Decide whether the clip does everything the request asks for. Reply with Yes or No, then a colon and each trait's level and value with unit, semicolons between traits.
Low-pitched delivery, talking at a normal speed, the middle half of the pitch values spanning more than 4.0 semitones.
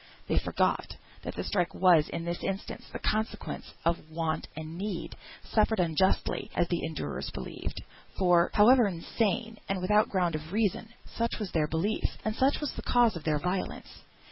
No: medium, 185 Hz; average, 170 wpm; average, 4.5 semitones